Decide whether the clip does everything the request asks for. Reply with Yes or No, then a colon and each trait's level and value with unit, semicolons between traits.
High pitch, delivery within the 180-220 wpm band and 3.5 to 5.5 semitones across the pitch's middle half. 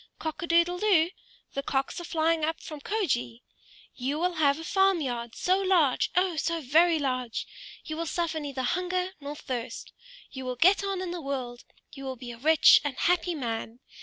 Yes: very high, 315 Hz; average, 190 wpm; average, 5.0 semitones